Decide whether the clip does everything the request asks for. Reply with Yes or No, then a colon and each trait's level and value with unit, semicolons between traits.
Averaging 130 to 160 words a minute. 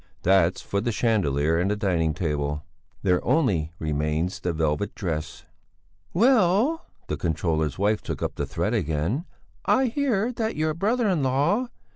Yes: average, 150 wpm